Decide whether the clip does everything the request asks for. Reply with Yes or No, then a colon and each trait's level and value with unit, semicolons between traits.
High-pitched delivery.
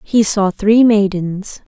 Yes: high, 205 Hz